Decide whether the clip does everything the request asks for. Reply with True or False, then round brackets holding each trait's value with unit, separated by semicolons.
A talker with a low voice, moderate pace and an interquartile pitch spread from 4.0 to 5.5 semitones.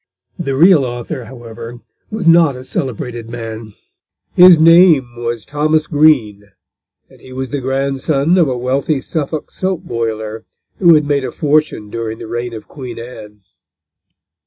True (130 Hz; 150 wpm; 4.8 semitones)